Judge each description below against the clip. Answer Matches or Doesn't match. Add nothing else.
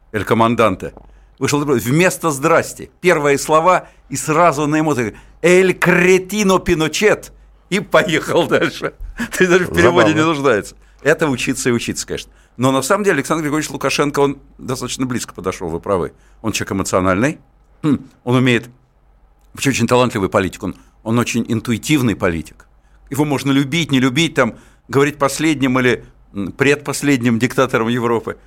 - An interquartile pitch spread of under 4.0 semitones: Doesn't match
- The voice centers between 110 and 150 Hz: Matches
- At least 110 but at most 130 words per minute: Doesn't match